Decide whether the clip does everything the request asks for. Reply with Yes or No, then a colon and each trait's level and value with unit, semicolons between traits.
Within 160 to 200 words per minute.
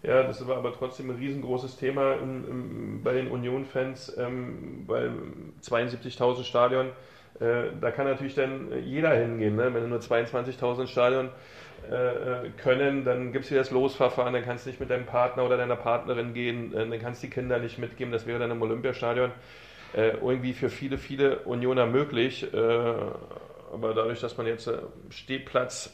Yes: average, 175 wpm